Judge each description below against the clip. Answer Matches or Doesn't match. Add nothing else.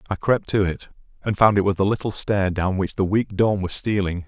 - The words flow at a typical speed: Doesn't match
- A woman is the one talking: Doesn't match